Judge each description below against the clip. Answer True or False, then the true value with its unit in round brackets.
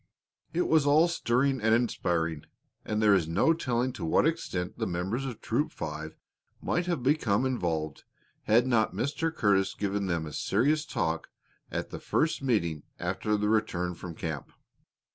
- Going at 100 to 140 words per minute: False (160 wpm)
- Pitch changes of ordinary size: False (7.4 semitones)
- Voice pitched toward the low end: True (105 Hz)